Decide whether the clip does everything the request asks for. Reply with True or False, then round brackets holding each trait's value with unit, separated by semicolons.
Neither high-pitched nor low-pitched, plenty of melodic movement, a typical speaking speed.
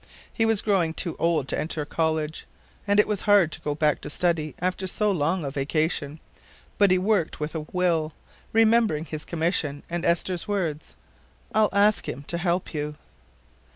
False (170 Hz; 4.1 semitones; 170 wpm)